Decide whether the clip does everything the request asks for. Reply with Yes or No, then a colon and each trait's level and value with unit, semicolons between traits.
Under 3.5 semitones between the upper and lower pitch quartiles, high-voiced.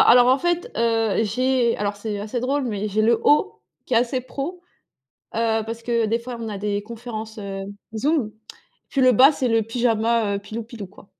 Yes: average, 2.8 semitones; high, 230 Hz